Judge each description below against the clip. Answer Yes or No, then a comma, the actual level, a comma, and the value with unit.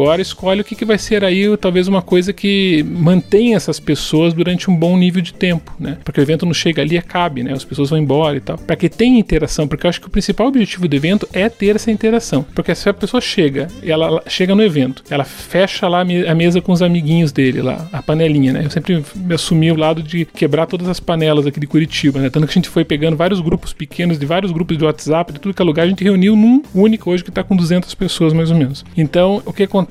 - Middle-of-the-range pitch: Yes, medium, 175 Hz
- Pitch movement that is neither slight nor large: Yes, average, 3.3 semitones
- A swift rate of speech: Yes, fast, 255 wpm